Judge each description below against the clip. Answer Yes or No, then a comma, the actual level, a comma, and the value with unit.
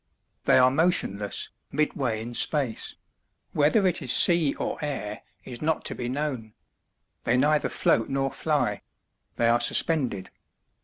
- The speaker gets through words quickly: No, average, 140 wpm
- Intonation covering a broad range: No, average, 4.5 semitones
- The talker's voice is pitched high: No, low, 130 Hz